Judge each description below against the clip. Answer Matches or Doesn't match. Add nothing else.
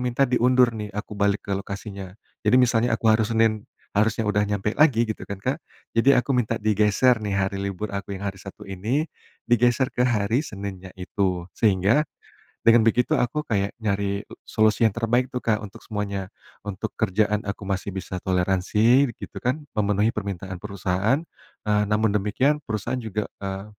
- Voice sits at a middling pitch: Doesn't match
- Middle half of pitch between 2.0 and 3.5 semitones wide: Matches